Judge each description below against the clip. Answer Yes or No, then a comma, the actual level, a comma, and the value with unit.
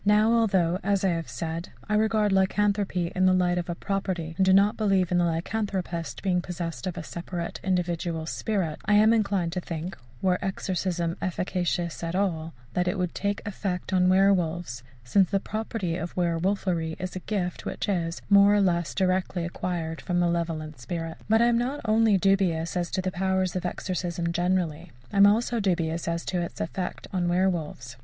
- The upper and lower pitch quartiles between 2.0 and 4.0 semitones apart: Yes, narrow, 2.6 semitones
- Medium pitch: Yes, medium, 180 Hz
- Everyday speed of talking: Yes, average, 190 wpm